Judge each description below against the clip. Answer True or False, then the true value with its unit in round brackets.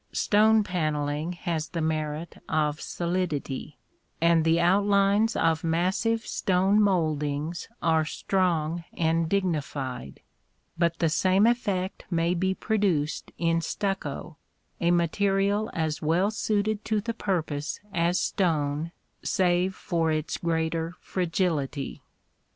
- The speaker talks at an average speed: False (110 wpm)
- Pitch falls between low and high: True (170 Hz)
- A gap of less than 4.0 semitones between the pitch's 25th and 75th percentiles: True (3.6 semitones)